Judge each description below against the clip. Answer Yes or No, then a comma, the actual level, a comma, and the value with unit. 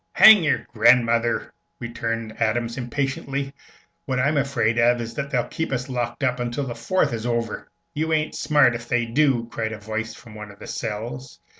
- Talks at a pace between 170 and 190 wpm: Yes, average, 185 wpm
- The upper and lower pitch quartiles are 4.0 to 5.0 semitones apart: No, average, 2.9 semitones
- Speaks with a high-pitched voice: No, low, 120 Hz